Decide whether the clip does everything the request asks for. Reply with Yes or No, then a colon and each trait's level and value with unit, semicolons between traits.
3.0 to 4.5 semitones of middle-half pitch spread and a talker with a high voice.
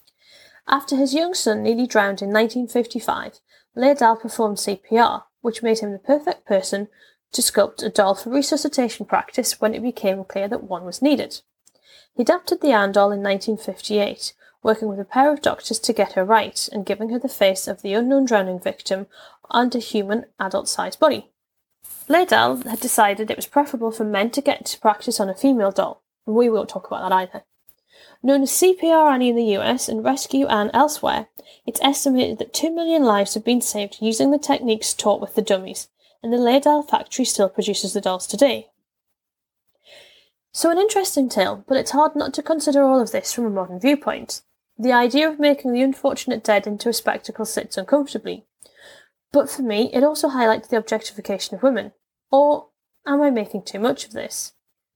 No: average, 5.1 semitones; high, 235 Hz